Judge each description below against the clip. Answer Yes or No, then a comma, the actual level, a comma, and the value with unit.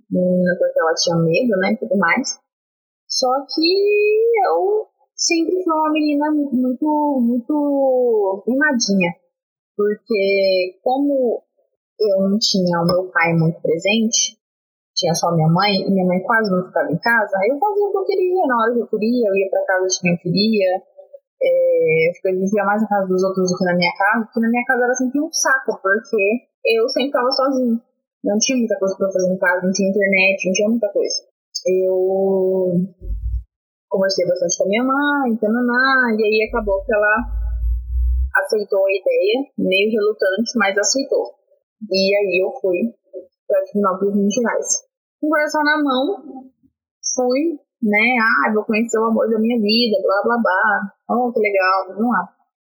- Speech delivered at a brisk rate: No, average, 175 wpm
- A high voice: Yes, high, 220 Hz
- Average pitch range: No, wide, 5.9 semitones